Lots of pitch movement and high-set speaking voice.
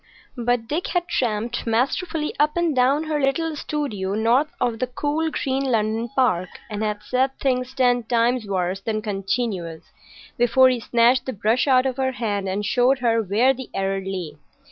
No: average, 4.0 semitones; high, 245 Hz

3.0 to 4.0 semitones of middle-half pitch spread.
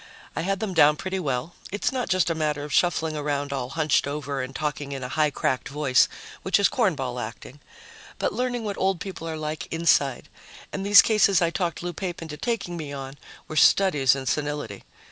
No: average, 4.8 semitones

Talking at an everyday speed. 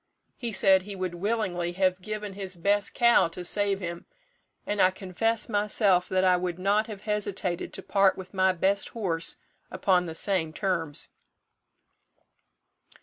Yes: average, 150 wpm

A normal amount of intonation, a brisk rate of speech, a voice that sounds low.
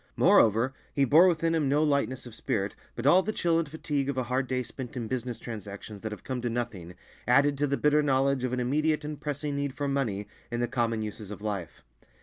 Yes: average, 3.9 semitones; fast, 230 wpm; low, 130 Hz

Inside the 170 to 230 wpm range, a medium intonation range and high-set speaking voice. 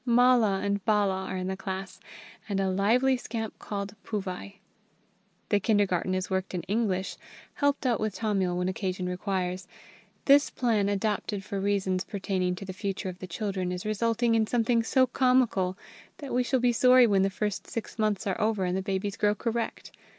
Yes: average, 180 wpm; average, 3.3 semitones; high, 200 Hz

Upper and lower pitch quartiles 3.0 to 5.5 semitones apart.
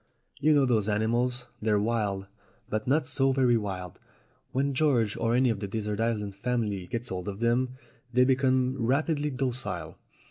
Yes: average, 3.8 semitones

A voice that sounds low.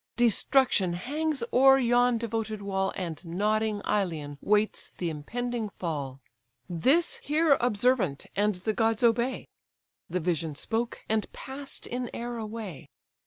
No: high, 220 Hz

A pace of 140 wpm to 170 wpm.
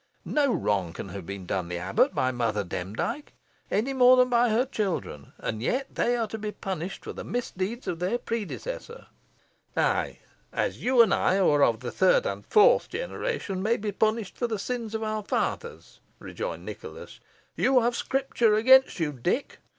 No: average, 185 wpm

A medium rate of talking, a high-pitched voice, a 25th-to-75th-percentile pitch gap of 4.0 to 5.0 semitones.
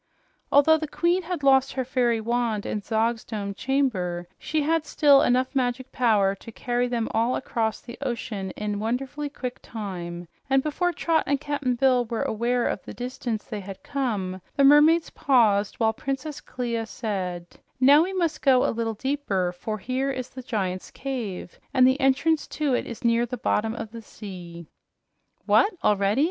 Yes: average, 175 wpm; high, 245 Hz; average, 4.3 semitones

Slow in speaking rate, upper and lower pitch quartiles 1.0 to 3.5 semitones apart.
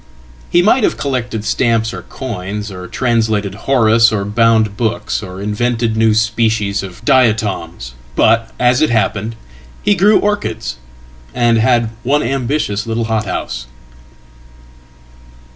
Yes: slow, 110 wpm; average, 2.7 semitones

